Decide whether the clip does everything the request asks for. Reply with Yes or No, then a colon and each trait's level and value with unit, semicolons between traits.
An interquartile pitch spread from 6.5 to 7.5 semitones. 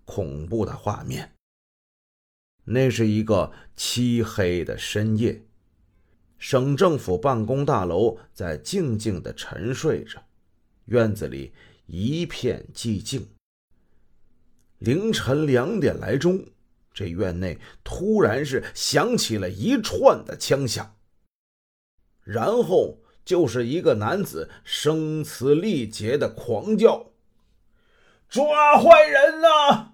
Yes: wide, 7.2 semitones